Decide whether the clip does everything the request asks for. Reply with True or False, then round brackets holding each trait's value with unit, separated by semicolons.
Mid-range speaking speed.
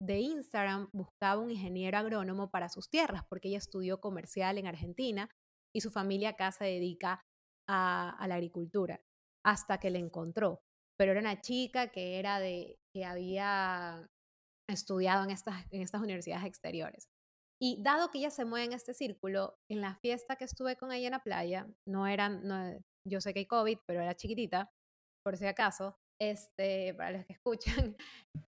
True (175 wpm)